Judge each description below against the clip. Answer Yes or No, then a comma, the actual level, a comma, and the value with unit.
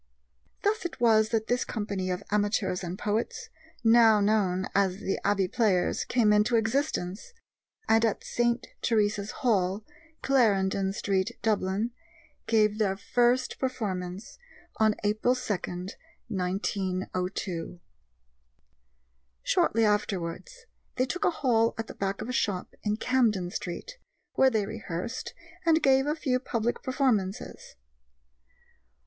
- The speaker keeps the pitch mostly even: No, average, 3.8 semitones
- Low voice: No, high, 215 Hz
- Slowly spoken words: Yes, slow, 120 wpm